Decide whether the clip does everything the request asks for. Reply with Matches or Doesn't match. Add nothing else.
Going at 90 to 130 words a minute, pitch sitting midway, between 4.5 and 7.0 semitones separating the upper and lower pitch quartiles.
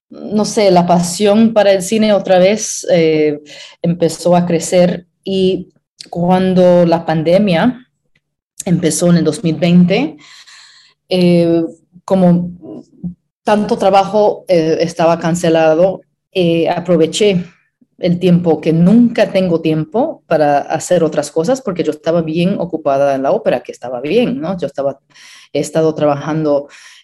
Doesn't match